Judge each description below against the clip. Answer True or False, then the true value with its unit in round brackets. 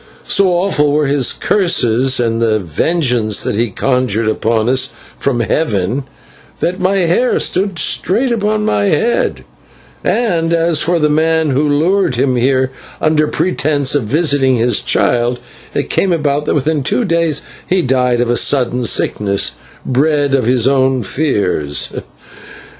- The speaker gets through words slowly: False (145 wpm)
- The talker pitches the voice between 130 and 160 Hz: True (140 Hz)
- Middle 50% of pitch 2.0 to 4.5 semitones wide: False (5.3 semitones)